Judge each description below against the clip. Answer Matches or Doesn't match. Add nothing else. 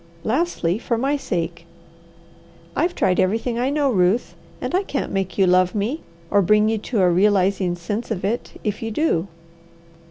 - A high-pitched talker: Matches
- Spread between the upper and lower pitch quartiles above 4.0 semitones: Matches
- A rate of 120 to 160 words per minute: Doesn't match